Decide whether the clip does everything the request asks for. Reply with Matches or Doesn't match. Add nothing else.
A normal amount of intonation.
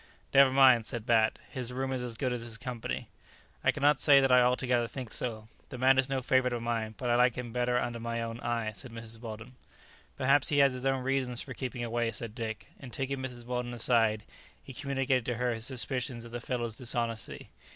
Doesn't match